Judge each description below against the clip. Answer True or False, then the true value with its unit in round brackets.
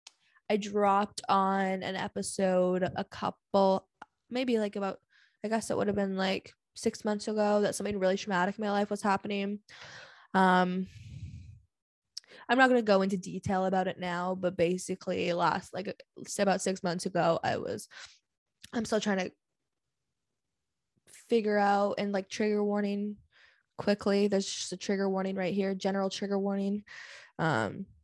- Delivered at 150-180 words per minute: True (155 wpm)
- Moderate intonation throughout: False (1.6 semitones)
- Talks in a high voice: True (195 Hz)